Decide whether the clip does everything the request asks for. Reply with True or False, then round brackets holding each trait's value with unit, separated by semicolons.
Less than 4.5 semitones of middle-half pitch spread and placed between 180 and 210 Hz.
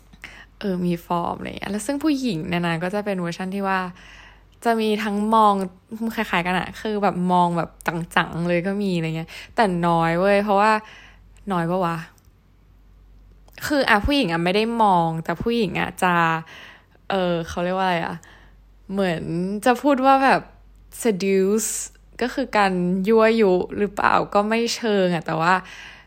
True (4.0 semitones; 185 Hz)